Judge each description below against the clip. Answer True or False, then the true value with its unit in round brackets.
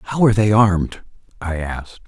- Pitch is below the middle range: True (100 Hz)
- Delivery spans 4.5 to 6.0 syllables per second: True (5.5 syllables/s)